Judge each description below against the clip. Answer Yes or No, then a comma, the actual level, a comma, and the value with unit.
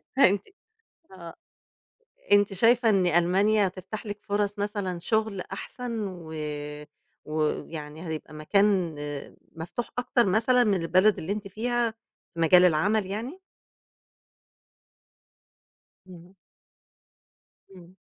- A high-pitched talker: Yes, high, 195 Hz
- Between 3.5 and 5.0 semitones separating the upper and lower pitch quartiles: Yes, average, 3.8 semitones